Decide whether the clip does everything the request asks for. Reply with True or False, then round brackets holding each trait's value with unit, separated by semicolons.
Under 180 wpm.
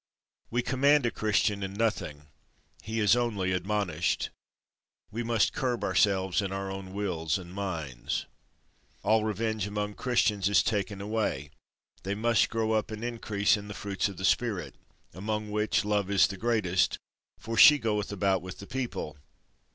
True (160 wpm)